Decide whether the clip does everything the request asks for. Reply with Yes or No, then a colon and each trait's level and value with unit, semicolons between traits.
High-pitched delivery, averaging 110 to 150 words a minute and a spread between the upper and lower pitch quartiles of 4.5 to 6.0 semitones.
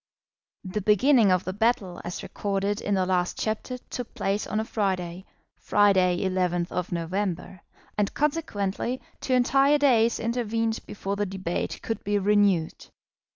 No: high, 205 Hz; average, 140 wpm; average, 3.4 semitones